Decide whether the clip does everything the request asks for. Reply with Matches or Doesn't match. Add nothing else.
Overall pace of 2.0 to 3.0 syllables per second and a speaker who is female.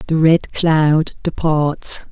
Matches